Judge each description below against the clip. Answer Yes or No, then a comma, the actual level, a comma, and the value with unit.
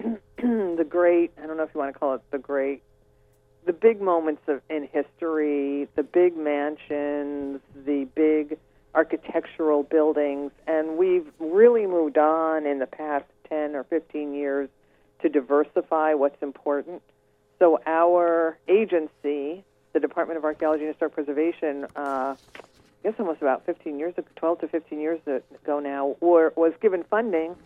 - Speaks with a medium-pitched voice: Yes, medium, 155 Hz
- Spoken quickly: No, average, 145 wpm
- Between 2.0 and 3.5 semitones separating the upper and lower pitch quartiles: Yes, average, 2.7 semitones